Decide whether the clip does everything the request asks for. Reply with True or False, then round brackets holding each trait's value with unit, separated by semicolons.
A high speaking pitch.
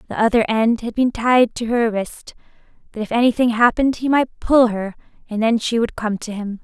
True (230 Hz)